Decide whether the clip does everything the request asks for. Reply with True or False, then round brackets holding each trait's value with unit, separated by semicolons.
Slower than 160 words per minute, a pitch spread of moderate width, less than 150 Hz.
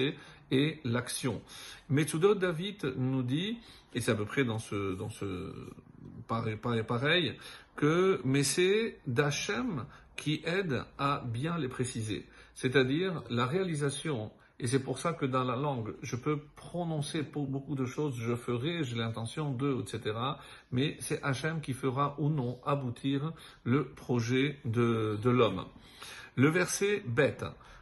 True (145 wpm; 3.7 semitones; 140 Hz)